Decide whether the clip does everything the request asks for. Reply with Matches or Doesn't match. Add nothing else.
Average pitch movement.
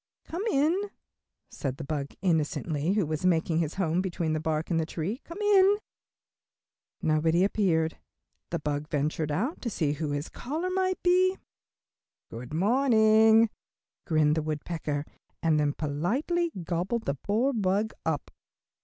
Doesn't match